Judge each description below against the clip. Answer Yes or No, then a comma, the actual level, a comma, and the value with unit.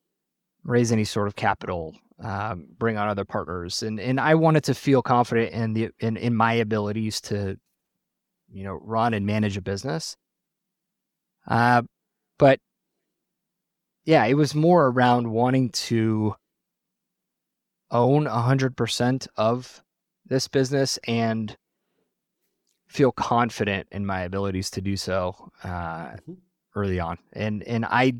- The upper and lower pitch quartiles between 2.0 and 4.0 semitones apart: No, average, 4.4 semitones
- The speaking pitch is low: Yes, low, 115 Hz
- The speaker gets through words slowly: Yes, slow, 130 wpm